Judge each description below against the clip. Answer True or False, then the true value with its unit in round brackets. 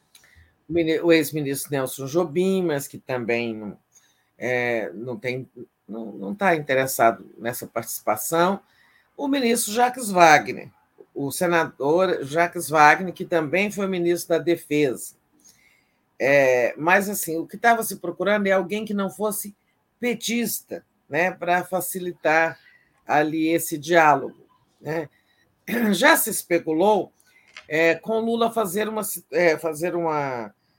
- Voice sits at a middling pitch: True (170 Hz)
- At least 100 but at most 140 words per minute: True (120 wpm)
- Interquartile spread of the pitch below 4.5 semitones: False (5.0 semitones)